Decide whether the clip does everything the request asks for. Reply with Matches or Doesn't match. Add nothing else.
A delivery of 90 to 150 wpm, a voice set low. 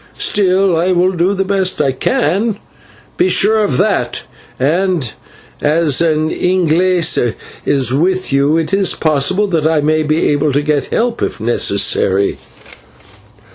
Doesn't match